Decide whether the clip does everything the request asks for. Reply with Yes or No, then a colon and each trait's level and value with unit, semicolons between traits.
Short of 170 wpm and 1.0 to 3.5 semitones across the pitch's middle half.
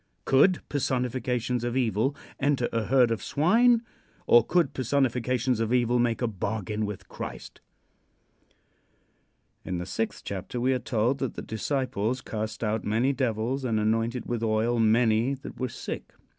Yes: average, 150 wpm; average, 2.9 semitones